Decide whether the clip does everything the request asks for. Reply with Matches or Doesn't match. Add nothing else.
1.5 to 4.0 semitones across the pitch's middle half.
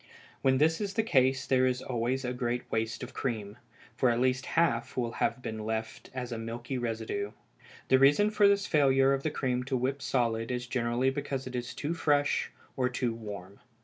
Matches